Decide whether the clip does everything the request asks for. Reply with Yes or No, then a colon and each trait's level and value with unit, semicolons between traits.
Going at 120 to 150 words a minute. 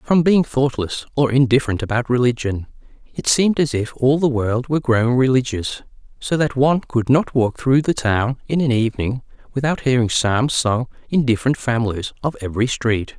No: average, 175 wpm